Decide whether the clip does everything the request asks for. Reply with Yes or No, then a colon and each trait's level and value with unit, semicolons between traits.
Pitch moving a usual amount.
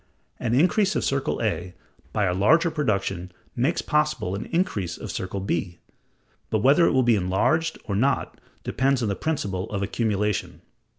No: wide, 7.4 semitones